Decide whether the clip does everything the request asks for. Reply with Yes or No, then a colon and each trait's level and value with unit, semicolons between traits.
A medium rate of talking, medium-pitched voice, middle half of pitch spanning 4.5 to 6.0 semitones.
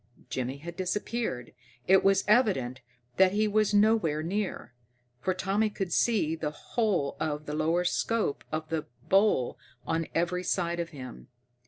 Yes: average, 150 wpm; medium, 175 Hz; average, 5.0 semitones